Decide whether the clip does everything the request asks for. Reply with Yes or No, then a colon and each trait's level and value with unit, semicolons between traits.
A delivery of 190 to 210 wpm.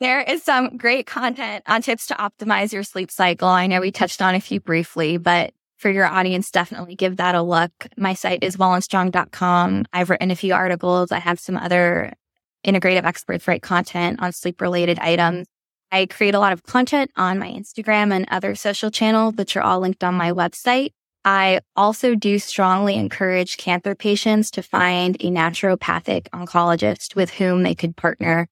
No: average, 180 wpm